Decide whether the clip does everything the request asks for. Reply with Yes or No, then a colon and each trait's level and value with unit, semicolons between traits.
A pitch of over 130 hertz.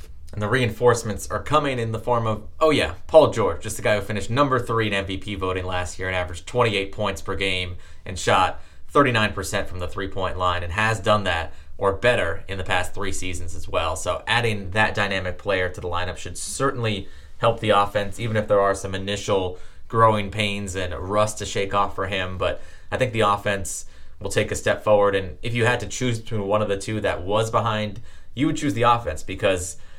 No: low, 100 Hz